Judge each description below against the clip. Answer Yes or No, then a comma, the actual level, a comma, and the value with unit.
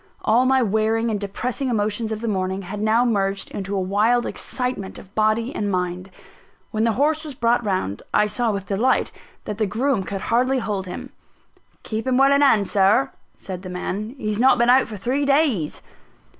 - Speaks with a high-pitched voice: Yes, high, 215 Hz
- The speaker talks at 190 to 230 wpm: Yes, average, 195 wpm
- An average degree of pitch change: Yes, average, 3.9 semitones